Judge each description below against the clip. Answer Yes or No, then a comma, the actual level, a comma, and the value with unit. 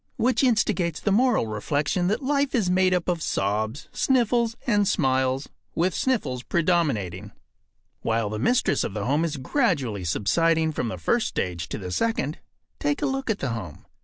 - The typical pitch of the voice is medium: Yes, medium, 160 Hz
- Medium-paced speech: Yes, average, 170 wpm